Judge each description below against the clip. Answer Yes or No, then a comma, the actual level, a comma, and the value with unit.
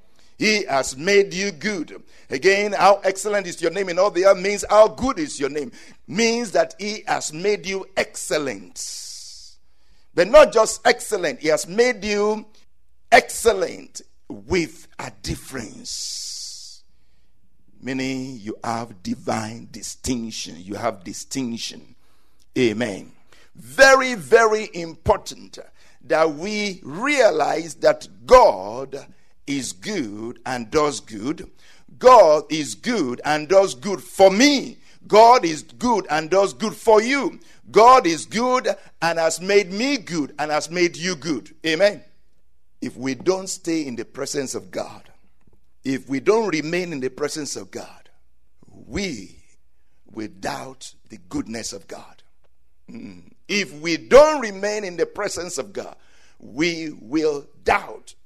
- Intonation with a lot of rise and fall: Yes, wide, 7.7 semitones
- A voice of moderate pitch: Yes, medium, 175 Hz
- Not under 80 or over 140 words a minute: Yes, slow, 135 wpm